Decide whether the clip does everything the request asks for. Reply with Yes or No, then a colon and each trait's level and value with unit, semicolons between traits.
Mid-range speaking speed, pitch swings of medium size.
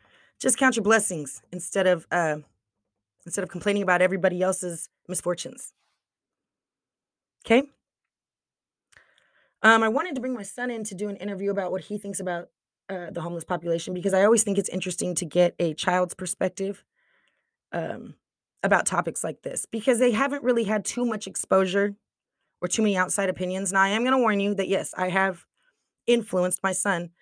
Yes: average, 175 wpm; average, 3.1 semitones